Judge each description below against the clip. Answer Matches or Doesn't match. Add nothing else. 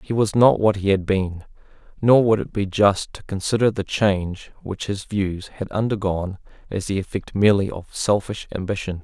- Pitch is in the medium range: Doesn't match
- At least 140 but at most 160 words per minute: Doesn't match